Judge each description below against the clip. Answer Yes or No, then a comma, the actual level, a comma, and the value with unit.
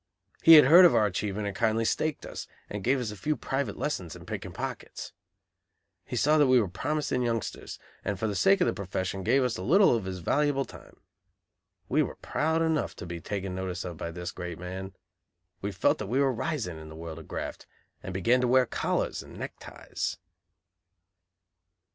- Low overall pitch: Yes, low, 110 Hz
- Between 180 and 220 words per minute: Yes, average, 200 wpm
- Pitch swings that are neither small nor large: No, wide, 6.8 semitones